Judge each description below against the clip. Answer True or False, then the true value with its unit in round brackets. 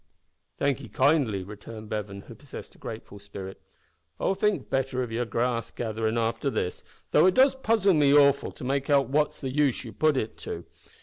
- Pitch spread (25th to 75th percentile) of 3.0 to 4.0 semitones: False (4.8 semitones)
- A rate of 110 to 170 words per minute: False (190 wpm)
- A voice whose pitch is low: True (130 Hz)